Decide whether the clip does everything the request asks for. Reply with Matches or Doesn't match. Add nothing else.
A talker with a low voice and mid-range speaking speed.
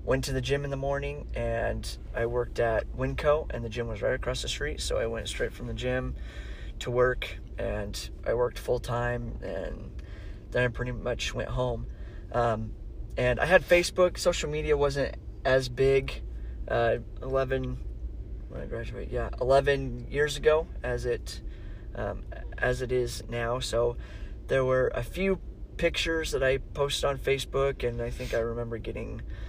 Matches